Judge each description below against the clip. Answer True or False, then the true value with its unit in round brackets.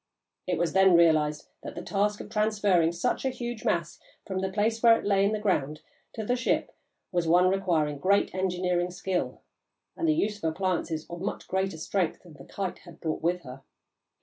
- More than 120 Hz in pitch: True (185 Hz)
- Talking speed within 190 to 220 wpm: True (200 wpm)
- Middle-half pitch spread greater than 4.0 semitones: False (3.4 semitones)